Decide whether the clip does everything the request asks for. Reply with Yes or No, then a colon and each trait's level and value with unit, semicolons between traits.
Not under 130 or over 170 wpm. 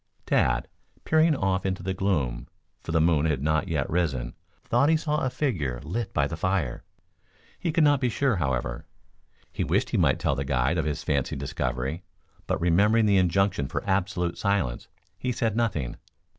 No: average, 180 wpm